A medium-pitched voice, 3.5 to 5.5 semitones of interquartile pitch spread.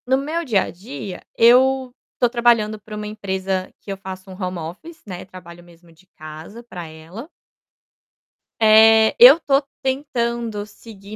No: high, 210 Hz; average, 4.5 semitones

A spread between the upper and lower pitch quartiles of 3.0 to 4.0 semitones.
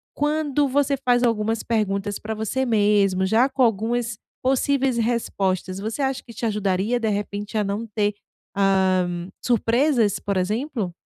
Yes: average, 3.7 semitones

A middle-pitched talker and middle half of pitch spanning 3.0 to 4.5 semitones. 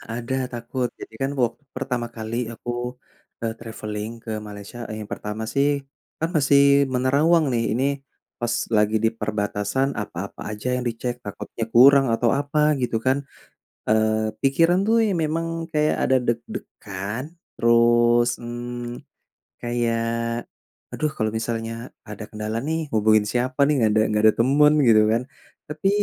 No: low, 120 Hz; average, 3.4 semitones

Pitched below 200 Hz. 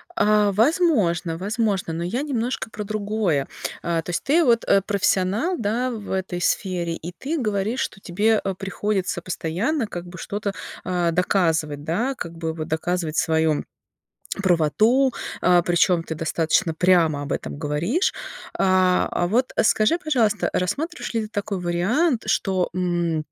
Yes: high, 190 Hz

